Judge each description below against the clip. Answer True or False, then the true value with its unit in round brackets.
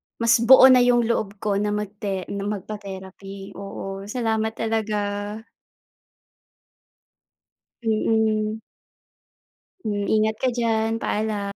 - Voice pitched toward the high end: True (215 Hz)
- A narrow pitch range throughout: True (1.9 semitones)